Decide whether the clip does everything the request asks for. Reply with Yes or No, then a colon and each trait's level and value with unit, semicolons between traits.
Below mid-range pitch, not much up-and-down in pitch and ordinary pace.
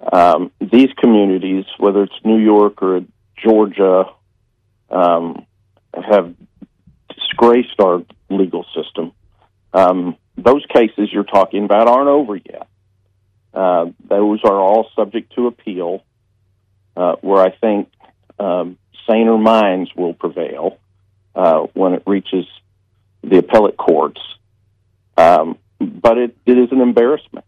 No: low, 100 Hz; narrow, 2.3 semitones; slow, 120 wpm